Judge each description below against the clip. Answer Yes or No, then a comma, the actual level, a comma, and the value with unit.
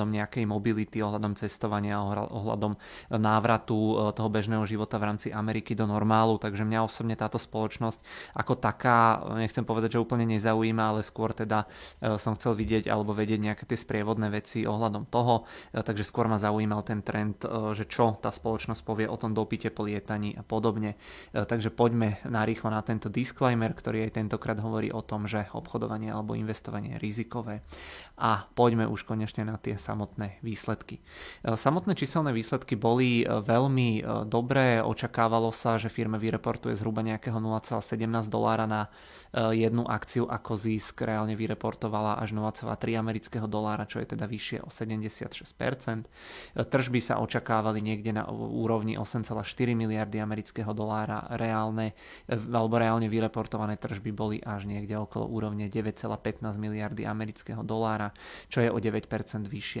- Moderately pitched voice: No, low, 110 Hz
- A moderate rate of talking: Yes, average, 145 wpm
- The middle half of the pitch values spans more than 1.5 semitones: No, narrow, 1.2 semitones